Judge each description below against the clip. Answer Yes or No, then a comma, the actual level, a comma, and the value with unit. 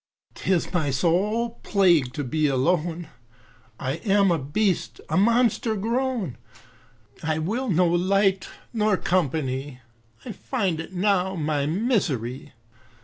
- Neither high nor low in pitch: Yes, medium, 180 Hz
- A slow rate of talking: Yes, slow, 120 wpm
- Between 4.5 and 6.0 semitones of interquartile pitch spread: Yes, average, 5.3 semitones